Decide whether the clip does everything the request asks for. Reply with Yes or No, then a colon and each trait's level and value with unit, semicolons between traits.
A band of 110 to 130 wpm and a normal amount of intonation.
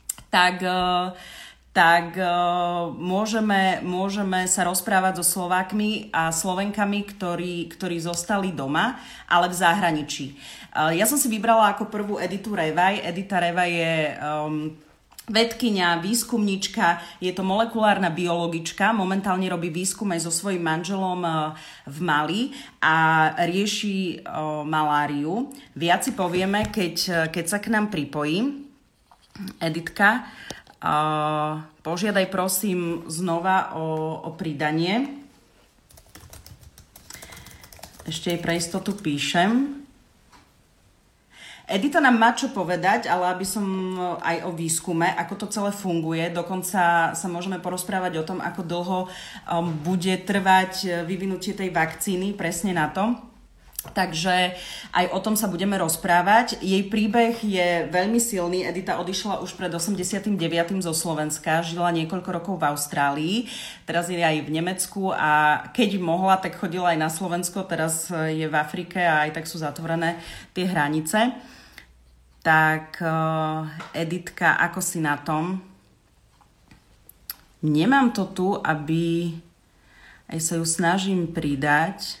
Yes: average, 115 wpm; average, 3.0 semitones